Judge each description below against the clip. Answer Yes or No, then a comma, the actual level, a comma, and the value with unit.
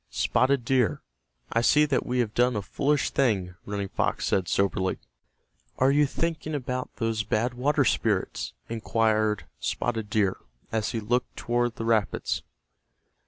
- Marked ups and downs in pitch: No, average, 3.1 semitones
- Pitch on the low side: Yes, low, 115 Hz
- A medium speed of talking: Yes, average, 145 wpm